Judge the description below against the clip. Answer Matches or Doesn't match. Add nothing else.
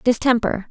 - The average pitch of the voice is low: Doesn't match